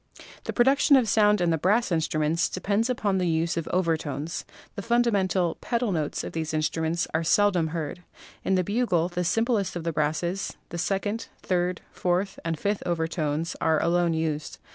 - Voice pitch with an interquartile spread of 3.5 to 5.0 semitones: Yes, average, 3.8 semitones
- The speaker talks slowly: No, average, 175 wpm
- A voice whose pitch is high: No, medium, 175 Hz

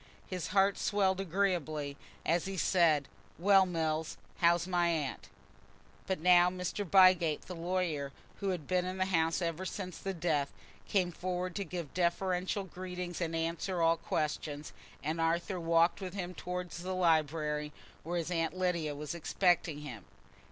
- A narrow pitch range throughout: Yes, narrow, 2.2 semitones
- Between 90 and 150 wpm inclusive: No, average, 160 wpm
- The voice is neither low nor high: Yes, medium, 175 Hz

